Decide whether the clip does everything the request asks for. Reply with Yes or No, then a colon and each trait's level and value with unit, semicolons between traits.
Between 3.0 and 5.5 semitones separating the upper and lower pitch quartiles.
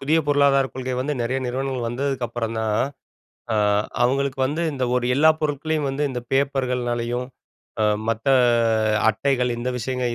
No: narrow, 2.4 semitones